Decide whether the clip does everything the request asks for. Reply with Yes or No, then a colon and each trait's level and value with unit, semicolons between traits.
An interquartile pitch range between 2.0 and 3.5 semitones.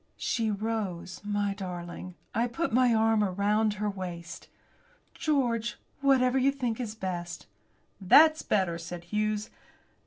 No: average, 4.2 semitones